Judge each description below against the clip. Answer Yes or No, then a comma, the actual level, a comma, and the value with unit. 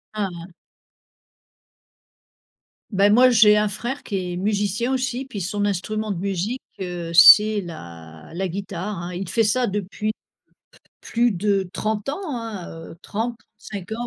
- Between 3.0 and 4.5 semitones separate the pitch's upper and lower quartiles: Yes, average, 3.5 semitones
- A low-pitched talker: No, high, 205 Hz